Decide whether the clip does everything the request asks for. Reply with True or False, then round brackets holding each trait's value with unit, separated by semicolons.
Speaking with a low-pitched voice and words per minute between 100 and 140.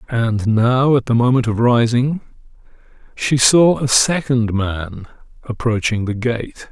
True (120 Hz; 135 wpm)